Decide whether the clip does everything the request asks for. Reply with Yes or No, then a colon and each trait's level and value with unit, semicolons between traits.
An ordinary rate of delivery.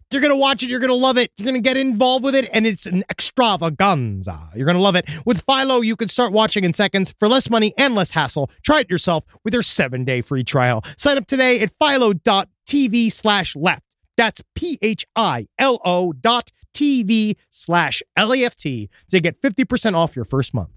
No: fast, 210 wpm